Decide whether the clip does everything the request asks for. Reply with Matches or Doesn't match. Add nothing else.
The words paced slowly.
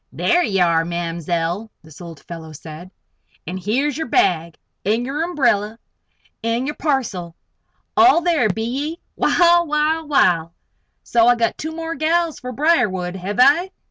Doesn't match